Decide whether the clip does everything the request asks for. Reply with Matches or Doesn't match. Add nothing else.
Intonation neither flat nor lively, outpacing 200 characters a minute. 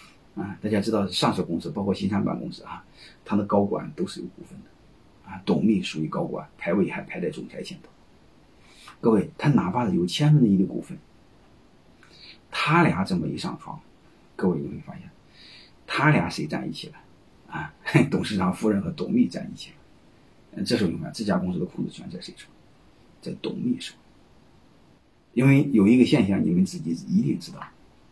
Doesn't match